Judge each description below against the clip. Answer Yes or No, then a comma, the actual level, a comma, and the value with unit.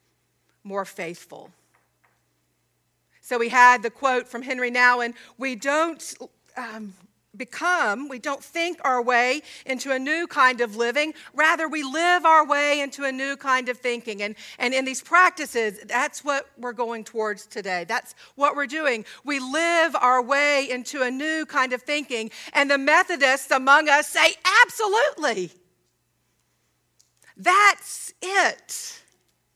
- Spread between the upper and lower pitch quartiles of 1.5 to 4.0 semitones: No, average, 4.4 semitones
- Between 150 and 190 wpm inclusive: No, average, 140 wpm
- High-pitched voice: Yes, very high, 265 Hz